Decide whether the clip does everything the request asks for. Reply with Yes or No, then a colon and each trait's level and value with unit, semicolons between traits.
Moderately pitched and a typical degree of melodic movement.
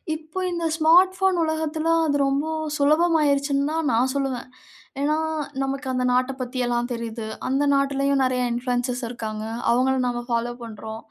No: very high, 275 Hz; average, 4.1 semitones